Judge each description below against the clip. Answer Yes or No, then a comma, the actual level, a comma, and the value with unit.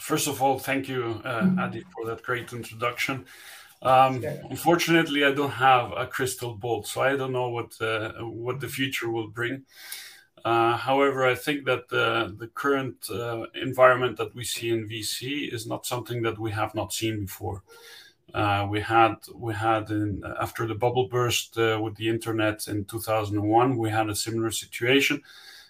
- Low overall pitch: Yes, low, 115 Hz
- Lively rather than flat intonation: No, average, 2.8 semitones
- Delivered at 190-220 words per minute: No, average, 180 wpm